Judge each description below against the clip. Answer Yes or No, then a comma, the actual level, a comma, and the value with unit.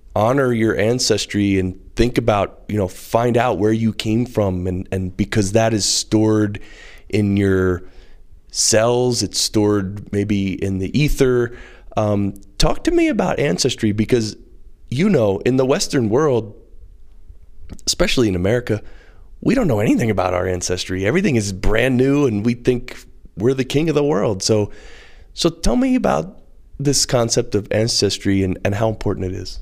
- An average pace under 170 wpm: Yes, average, 160 wpm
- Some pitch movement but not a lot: Yes, average, 4.1 semitones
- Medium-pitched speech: No, low, 105 Hz